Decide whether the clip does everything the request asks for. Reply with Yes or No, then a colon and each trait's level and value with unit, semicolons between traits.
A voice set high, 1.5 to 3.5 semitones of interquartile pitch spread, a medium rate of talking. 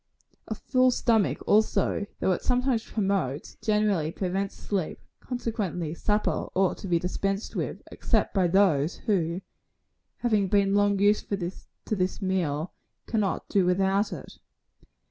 No: high, 195 Hz; average, 2.8 semitones; slow, 130 wpm